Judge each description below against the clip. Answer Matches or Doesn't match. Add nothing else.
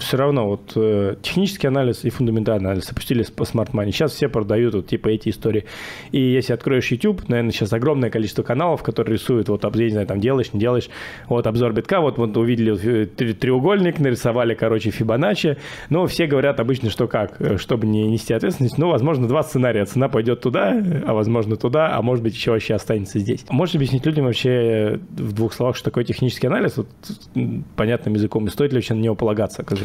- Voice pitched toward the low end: Matches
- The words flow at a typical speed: Doesn't match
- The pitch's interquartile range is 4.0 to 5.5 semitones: Doesn't match